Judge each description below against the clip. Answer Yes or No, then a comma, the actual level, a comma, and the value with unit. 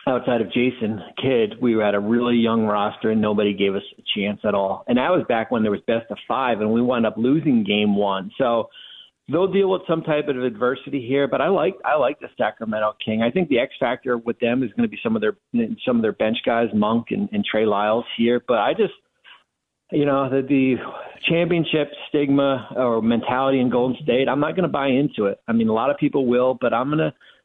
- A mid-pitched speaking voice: No, low, 125 Hz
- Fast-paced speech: Yes, fast, 235 wpm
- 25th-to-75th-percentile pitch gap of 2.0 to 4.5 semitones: No, average, 5.1 semitones